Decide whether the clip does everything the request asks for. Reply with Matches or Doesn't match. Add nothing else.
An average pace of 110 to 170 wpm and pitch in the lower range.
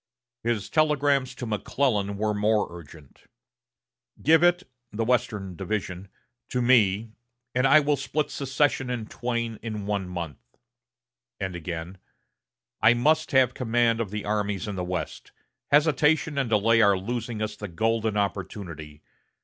Matches